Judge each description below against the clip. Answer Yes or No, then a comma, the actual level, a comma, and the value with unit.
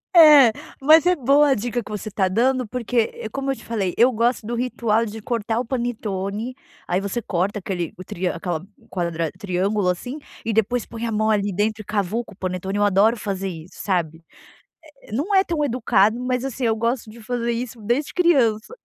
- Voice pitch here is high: Yes, high, 225 Hz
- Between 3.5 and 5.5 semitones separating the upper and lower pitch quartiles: Yes, average, 3.9 semitones